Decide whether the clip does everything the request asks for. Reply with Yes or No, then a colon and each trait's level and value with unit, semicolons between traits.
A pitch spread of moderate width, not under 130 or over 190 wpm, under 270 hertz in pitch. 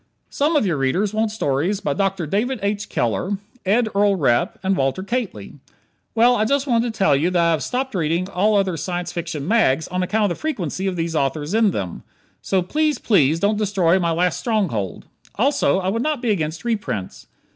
No: average, 4.9 semitones; average, 200 wpm; high, 190 Hz